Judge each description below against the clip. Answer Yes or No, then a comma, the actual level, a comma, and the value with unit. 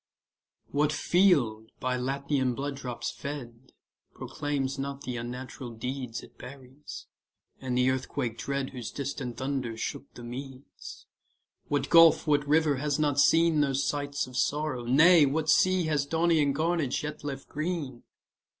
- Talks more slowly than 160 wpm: Yes, average, 140 wpm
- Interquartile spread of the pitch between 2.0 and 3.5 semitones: Yes, average, 2.7 semitones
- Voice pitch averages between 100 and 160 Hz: Yes, medium, 140 Hz